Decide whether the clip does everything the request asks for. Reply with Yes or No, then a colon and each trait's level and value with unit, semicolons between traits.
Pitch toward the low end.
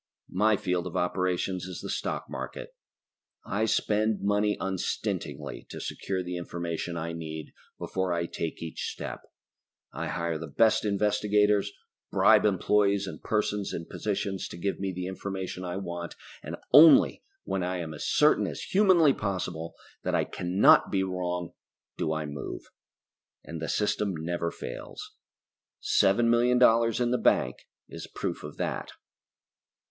Yes: very low, 95 Hz